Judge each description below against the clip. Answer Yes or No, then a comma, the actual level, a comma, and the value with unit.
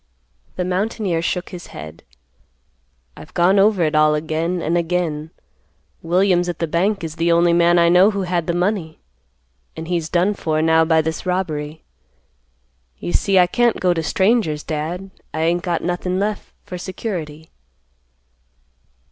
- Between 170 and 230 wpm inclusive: No, average, 155 wpm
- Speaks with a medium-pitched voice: Yes, medium, 175 Hz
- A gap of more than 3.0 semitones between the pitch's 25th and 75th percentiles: No, narrow, 2.4 semitones